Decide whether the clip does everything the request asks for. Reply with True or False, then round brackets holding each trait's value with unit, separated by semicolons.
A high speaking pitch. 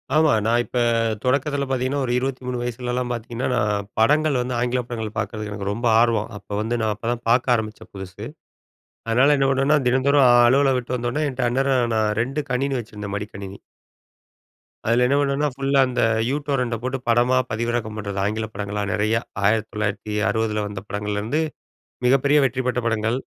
False (120 Hz)